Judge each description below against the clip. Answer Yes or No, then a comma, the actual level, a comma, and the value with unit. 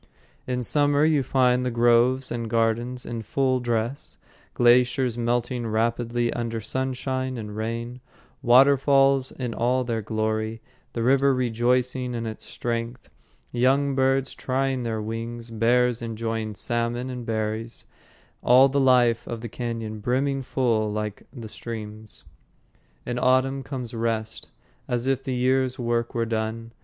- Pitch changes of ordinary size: No, narrow, 2.2 semitones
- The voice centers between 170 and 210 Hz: No, low, 120 Hz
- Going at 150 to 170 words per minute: No, slow, 135 wpm